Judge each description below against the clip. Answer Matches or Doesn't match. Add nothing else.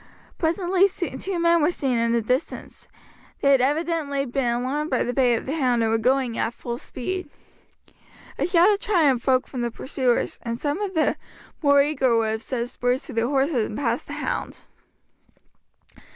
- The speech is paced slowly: Doesn't match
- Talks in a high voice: Matches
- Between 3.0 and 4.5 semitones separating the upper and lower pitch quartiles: Doesn't match